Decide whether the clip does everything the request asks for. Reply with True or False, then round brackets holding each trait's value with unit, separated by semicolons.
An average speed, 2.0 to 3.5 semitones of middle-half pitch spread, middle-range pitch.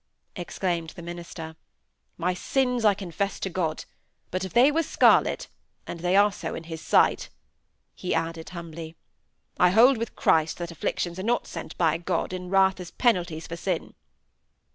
True (165 wpm; 2.7 semitones; 180 Hz)